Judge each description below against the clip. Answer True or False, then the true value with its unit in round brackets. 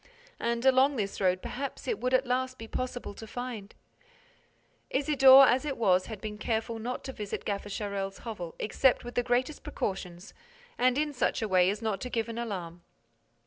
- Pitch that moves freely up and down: False (4.2 semitones)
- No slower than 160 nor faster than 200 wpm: True (185 wpm)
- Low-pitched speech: False (230 Hz)